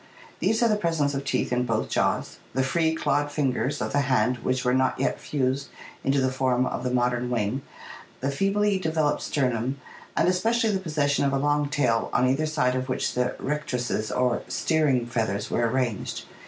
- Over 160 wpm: Yes, average, 190 wpm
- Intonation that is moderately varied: Yes, average, 3.2 semitones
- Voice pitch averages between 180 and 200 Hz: No, low, 135 Hz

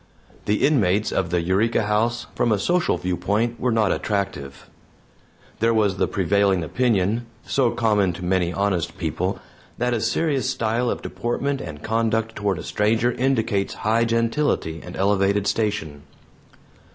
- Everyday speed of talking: Yes, average, 145 wpm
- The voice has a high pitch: No, low, 105 Hz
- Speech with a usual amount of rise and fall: Yes, average, 3.7 semitones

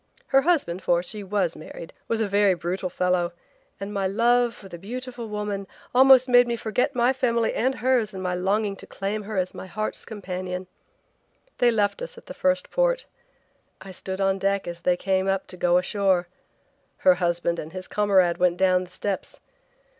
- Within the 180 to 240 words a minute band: Yes, average, 190 wpm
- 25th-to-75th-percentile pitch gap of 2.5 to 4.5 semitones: Yes, average, 4.2 semitones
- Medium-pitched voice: No, high, 195 Hz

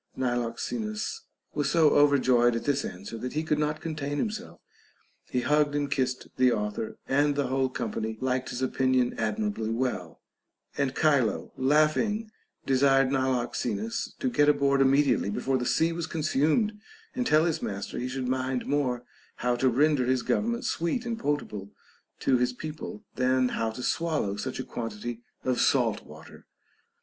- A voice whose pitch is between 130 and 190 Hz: Yes, low, 135 Hz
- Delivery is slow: No, average, 160 wpm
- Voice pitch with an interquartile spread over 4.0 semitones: No, average, 3.6 semitones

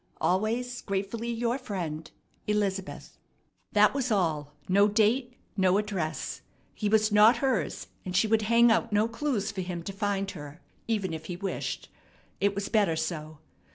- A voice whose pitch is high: Yes, high, 205 Hz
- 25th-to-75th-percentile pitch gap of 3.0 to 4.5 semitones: Yes, average, 3.5 semitones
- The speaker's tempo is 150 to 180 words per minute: Yes, average, 155 wpm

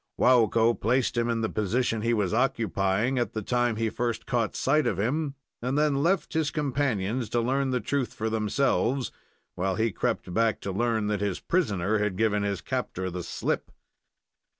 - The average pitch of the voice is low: Yes, low, 115 Hz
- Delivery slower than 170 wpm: No, average, 180 wpm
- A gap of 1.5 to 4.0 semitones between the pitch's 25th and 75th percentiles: Yes, average, 3.6 semitones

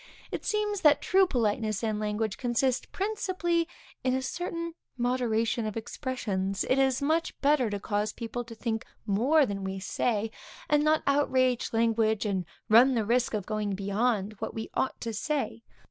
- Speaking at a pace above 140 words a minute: Yes, average, 165 wpm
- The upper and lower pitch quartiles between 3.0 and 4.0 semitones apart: No, average, 4.6 semitones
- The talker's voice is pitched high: Yes, high, 235 Hz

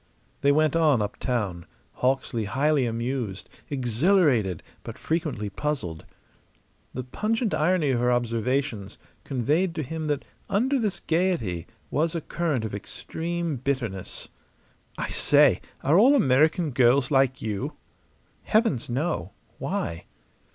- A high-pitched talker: No, low, 135 Hz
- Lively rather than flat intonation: Yes, wide, 5.8 semitones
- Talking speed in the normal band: No, slow, 120 wpm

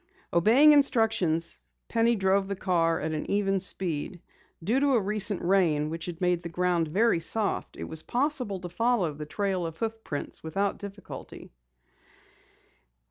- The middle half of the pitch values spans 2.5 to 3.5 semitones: No, average, 4.8 semitones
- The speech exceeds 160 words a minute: No, average, 155 wpm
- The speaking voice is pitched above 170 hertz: Yes, high, 190 Hz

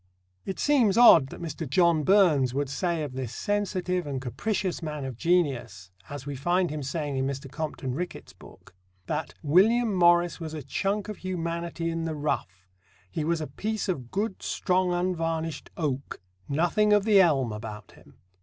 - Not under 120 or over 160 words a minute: No, average, 175 wpm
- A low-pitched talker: No, medium, 165 Hz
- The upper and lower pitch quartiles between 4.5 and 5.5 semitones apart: Yes, average, 4.9 semitones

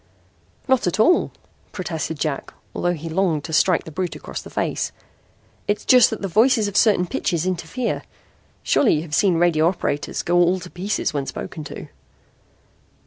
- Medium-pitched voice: Yes, medium, 175 Hz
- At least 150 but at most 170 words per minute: Yes, average, 165 wpm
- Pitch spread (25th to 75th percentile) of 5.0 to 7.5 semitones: No, average, 3.9 semitones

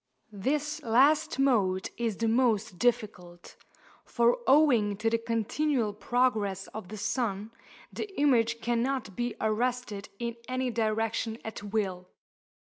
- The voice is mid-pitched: No, high, 230 Hz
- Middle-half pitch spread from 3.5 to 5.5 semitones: No, average, 3.0 semitones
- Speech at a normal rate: No, slow, 125 wpm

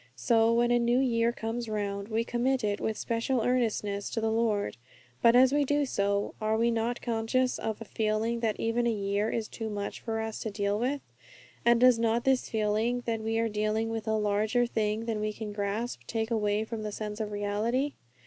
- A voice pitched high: Yes, high, 225 Hz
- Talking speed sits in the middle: No, fast, 210 wpm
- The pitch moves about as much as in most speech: No, narrow, 1.9 semitones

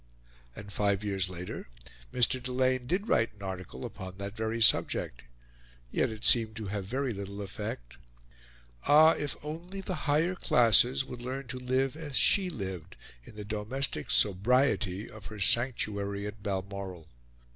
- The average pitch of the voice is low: Yes, low, 110 Hz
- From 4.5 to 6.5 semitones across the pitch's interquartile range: Yes, average, 4.8 semitones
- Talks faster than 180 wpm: No, average, 150 wpm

